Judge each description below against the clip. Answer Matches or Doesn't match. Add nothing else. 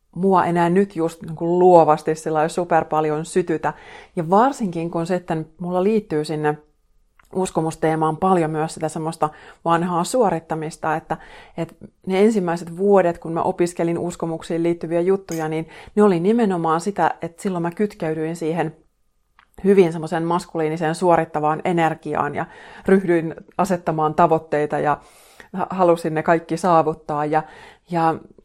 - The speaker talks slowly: Doesn't match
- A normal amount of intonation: Doesn't match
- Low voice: Doesn't match